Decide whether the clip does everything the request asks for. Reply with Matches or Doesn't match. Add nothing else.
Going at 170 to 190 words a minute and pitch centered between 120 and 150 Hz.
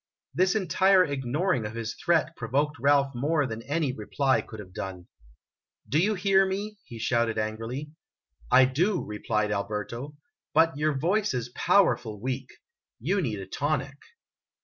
Doesn't match